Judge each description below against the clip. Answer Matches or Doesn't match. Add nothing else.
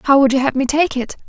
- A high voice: Matches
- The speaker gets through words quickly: Matches